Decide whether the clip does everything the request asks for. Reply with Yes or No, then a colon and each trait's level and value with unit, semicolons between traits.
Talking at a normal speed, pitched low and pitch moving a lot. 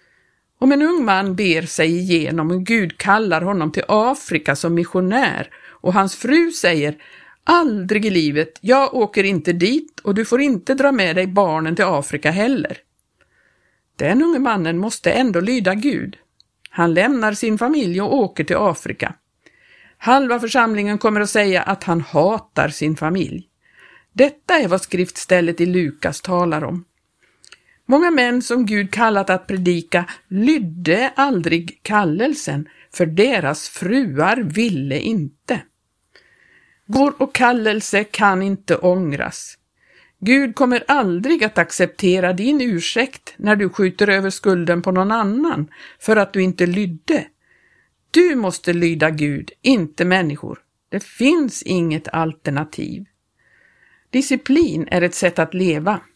No: average, 135 wpm; high, 195 Hz; wide, 6.3 semitones